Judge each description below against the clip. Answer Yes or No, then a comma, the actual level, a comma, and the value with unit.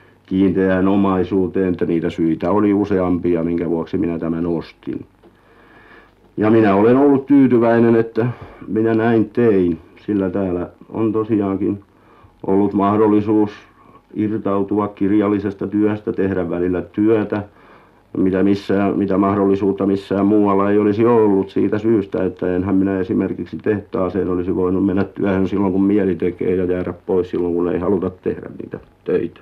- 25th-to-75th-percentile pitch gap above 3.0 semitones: No, narrow, 2.4 semitones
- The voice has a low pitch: Yes, low, 100 Hz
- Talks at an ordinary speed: Yes, average, 135 wpm